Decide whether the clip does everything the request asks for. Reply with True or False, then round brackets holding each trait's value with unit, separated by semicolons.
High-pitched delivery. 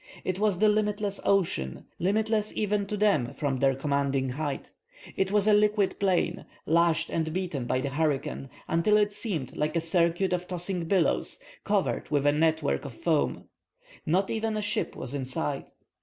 False (170 Hz)